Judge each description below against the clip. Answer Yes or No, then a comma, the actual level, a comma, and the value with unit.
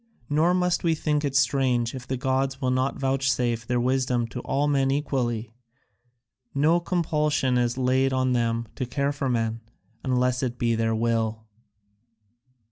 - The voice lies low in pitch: Yes, low, 130 Hz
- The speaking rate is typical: Yes, average, 155 wpm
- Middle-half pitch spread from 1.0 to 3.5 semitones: Yes, narrow, 2.5 semitones